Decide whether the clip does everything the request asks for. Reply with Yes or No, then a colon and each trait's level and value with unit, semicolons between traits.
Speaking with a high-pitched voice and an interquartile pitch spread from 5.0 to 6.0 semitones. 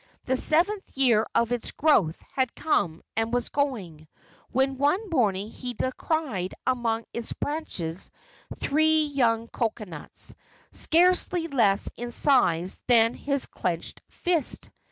Yes: high, 245 Hz; wide, 5.4 semitones